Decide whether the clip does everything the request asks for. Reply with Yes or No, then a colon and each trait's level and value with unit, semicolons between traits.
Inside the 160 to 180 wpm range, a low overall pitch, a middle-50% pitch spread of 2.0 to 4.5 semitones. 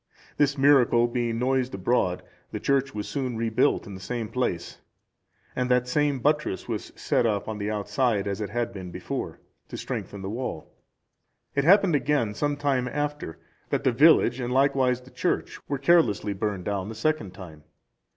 No: average, 175 wpm; low, 120 Hz; average, 5.0 semitones